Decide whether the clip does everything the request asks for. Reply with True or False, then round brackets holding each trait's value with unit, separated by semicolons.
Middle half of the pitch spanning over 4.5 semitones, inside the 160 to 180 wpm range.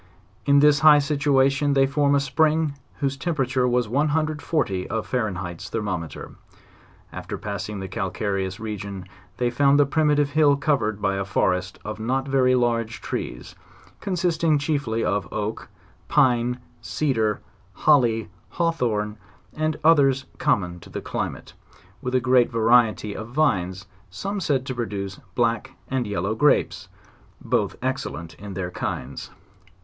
False (5.6 semitones; 135 wpm)